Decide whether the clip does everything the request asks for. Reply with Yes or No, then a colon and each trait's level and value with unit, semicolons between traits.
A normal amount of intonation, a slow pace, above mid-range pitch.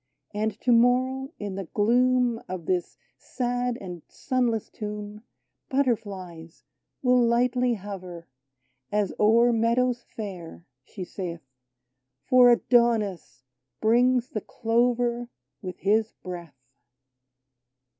Yes: average, 4.7 semitones; slow, 105 wpm; high, 220 Hz